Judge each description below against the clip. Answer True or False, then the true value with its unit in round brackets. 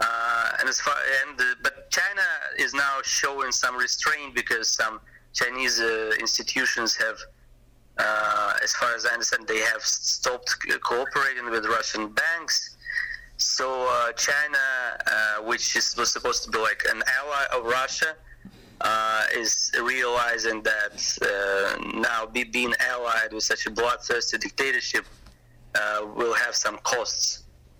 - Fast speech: False (140 wpm)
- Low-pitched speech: True (115 Hz)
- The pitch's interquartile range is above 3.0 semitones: False (2.7 semitones)